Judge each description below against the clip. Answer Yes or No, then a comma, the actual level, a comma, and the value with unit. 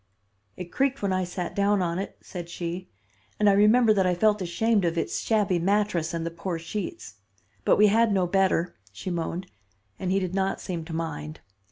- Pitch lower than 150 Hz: No, medium, 185 Hz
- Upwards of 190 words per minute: Yes, average, 200 wpm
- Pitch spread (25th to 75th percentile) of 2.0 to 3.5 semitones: Yes, average, 3.2 semitones